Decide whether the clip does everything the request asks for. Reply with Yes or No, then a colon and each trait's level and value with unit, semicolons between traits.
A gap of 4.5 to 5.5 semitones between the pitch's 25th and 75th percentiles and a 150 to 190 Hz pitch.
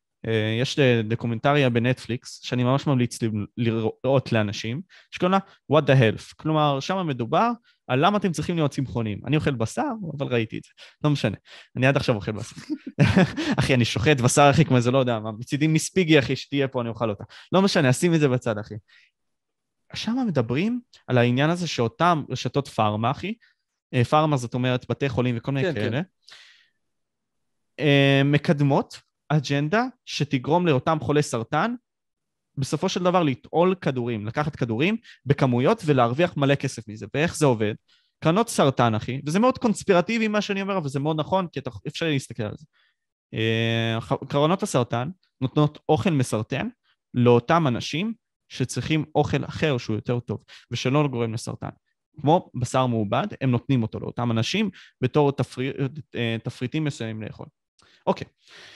No: average, 5.1 semitones; medium, 140 Hz